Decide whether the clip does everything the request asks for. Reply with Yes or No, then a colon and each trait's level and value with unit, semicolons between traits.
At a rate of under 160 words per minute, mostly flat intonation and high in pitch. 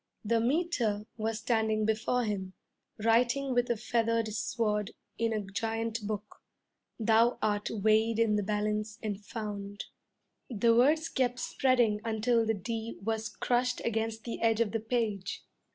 Yes: average, 150 wpm; narrow, 1.7 semitones; high, 225 Hz